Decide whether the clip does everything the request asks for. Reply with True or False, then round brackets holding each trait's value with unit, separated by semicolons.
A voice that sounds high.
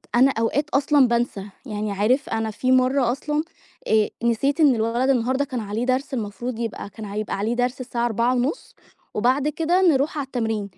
True (245 Hz)